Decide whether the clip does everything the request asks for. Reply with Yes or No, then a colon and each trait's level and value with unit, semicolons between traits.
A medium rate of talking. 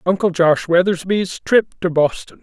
Yes: average, 150 wpm